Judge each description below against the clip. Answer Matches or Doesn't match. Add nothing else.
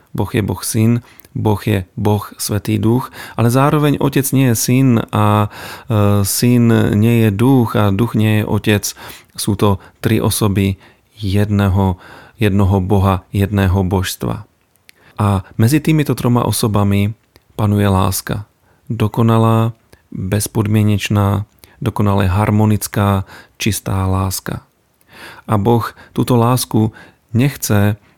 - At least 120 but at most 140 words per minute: Doesn't match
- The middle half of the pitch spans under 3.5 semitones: Matches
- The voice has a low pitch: Matches